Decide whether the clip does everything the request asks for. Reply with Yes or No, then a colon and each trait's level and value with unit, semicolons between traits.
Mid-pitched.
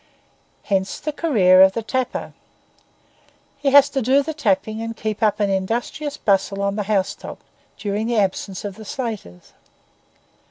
No: high, 215 Hz